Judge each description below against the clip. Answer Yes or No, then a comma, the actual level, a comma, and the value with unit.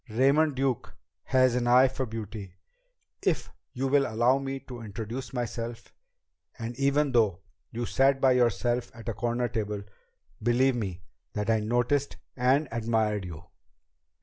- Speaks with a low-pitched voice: Yes, low, 120 Hz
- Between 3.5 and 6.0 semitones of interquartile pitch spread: No, average, 3.0 semitones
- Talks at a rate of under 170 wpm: Yes, average, 145 wpm